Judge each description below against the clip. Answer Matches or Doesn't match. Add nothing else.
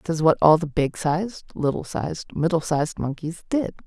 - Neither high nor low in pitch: Matches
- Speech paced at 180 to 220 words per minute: Matches